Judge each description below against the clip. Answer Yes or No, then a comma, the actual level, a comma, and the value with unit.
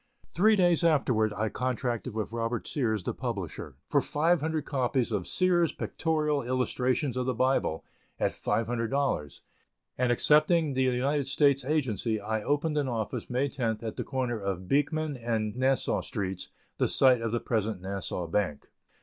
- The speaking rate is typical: Yes, average, 160 wpm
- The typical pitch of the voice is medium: No, low, 125 Hz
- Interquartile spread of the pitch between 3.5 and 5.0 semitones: Yes, average, 4.6 semitones